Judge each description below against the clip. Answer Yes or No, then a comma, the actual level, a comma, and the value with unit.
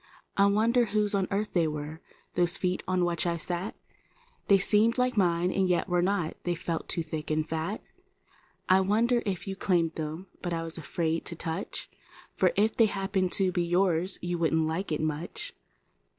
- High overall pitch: No, medium, 180 Hz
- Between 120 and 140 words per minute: No, average, 170 wpm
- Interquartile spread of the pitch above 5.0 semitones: No, average, 3.2 semitones